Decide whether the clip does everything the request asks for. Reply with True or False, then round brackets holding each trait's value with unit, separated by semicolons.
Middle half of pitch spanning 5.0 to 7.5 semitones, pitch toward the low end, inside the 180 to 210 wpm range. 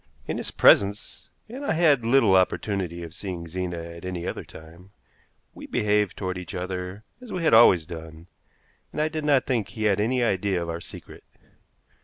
True (5.3 semitones; 95 Hz; 185 wpm)